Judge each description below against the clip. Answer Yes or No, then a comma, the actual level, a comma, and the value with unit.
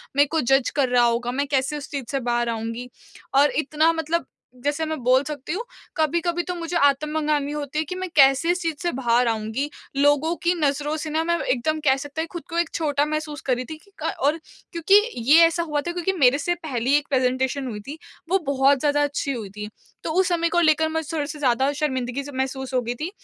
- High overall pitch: Yes, very high, 290 Hz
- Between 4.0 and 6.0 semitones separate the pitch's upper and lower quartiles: No, average, 3.4 semitones